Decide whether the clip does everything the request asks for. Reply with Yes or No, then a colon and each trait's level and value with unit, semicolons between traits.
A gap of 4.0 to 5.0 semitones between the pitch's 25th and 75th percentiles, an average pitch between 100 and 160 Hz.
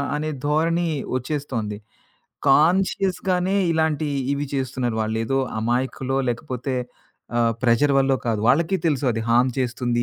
Yes: average, 4.5 semitones; low, 135 Hz